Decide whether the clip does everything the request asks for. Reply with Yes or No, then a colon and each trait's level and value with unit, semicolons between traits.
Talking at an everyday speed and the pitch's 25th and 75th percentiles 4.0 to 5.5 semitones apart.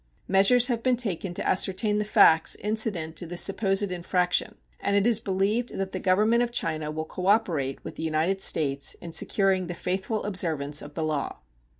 Yes: average, 185 wpm; average, 4.4 semitones